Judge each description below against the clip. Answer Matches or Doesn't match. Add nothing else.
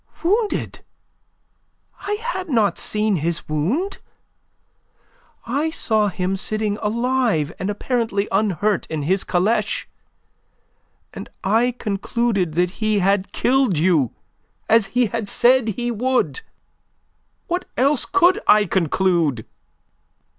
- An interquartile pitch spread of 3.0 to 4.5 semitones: Doesn't match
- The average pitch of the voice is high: Matches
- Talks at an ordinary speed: Doesn't match